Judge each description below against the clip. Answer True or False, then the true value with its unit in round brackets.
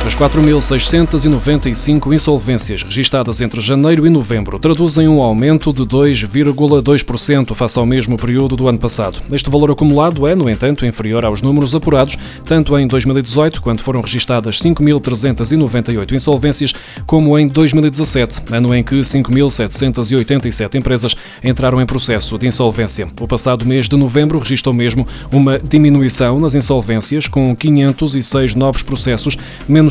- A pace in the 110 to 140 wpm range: True (135 wpm)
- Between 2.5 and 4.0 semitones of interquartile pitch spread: True (3.2 semitones)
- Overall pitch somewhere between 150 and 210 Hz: False (135 Hz)